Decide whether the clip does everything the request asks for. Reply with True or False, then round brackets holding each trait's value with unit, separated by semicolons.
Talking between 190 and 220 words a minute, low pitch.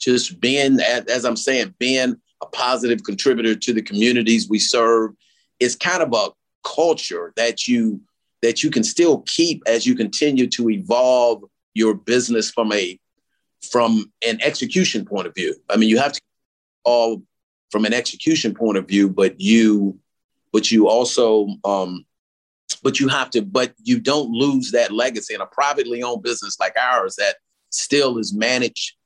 False (165 wpm; 120 Hz)